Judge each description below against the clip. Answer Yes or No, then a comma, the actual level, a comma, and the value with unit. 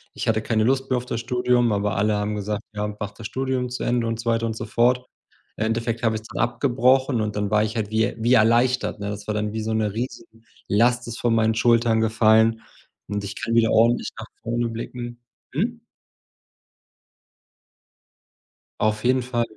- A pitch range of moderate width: No, narrow, 2.0 semitones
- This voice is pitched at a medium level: No, low, 115 Hz